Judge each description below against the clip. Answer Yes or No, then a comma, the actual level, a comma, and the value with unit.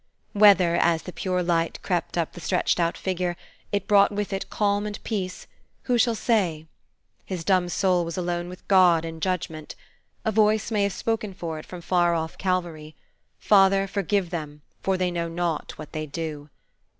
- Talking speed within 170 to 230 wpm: Yes, average, 180 wpm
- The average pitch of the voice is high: No, medium, 180 Hz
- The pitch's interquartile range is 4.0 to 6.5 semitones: No, average, 3.0 semitones